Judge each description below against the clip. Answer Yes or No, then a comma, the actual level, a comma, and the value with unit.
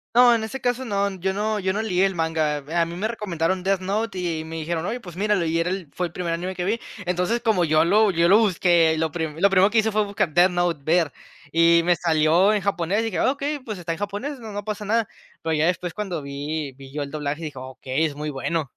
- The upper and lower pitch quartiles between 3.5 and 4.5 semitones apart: Yes, average, 4.2 semitones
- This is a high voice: No, medium, 180 Hz